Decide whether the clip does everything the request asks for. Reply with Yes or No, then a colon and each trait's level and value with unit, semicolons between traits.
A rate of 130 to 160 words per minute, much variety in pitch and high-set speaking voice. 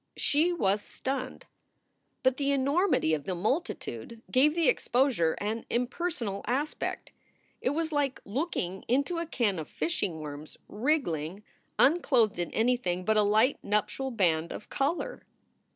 Yes: average, 140 wpm; wide, 6.7 semitones; high, 245 Hz